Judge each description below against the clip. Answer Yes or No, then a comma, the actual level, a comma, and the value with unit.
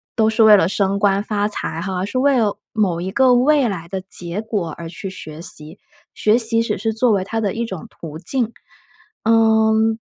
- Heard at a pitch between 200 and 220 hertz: Yes, high, 210 Hz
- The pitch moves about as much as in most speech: Yes, average, 3.3 semitones